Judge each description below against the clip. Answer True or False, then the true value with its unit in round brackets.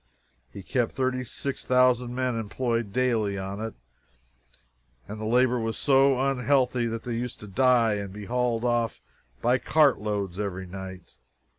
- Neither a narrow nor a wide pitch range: True (3.4 semitones)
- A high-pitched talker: False (120 Hz)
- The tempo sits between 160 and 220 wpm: False (140 wpm)